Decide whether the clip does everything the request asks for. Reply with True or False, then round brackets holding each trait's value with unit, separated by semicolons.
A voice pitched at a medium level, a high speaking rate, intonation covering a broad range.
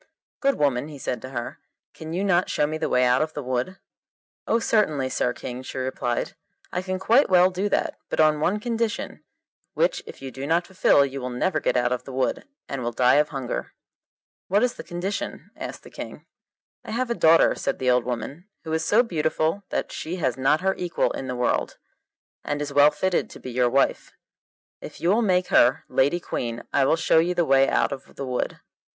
True (150 Hz; 220 wpm; 5.9 semitones)